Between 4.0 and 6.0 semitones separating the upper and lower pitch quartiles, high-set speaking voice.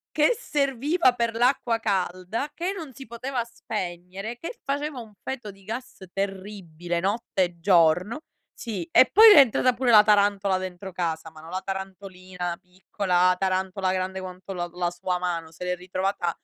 Yes: average, 4.7 semitones; high, 195 Hz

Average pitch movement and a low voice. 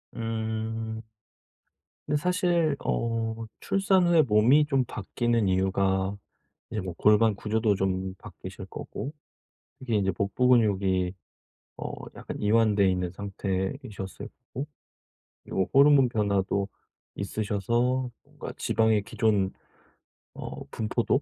Yes: average, 4.2 semitones; low, 110 Hz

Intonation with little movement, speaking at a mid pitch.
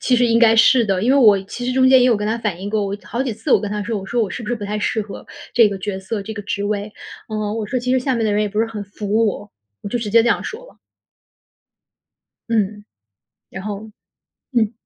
No: narrow, 2.3 semitones; high, 215 Hz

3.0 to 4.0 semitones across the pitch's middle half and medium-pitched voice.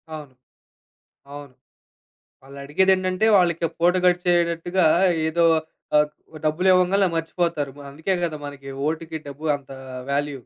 Yes: average, 3.5 semitones; medium, 165 Hz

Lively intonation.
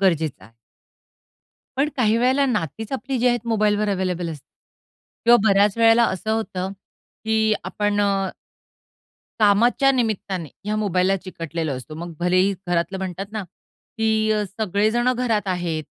No: average, 3.5 semitones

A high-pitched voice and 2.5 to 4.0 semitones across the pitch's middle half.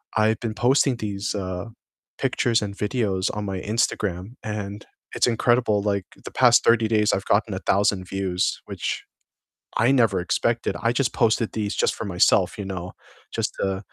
No: low, 105 Hz; average, 2.9 semitones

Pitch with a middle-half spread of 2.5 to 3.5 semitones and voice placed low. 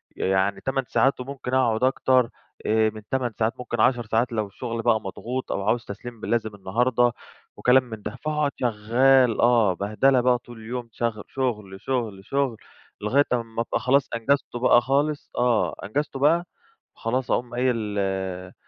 Yes: average, 3.0 semitones; low, 120 Hz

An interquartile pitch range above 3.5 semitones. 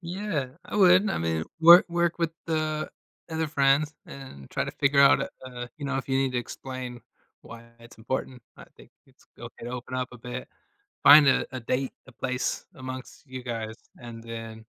Yes: average, 3.9 semitones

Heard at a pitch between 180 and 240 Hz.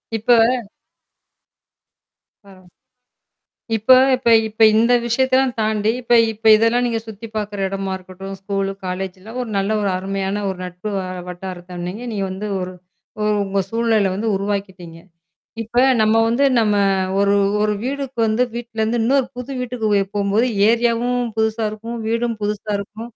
Yes: high, 215 Hz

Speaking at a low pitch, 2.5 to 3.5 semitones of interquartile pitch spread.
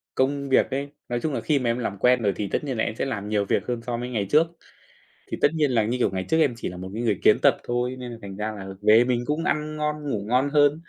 No: low, 125 Hz; average, 4.7 semitones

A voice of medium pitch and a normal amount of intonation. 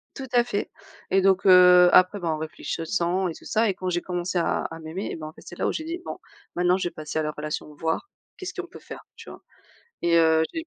Yes: medium, 180 Hz; average, 3.2 semitones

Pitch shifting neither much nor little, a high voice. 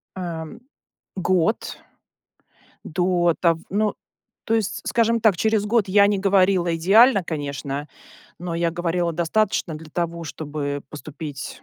No: average, 3.9 semitones; medium, 175 Hz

